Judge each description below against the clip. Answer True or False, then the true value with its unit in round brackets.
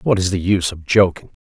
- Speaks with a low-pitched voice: True (95 Hz)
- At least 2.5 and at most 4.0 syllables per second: False (6.5 syllables/s)